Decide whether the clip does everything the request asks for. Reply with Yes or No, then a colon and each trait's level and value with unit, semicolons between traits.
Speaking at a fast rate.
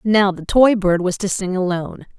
Yes: fast, 220 wpm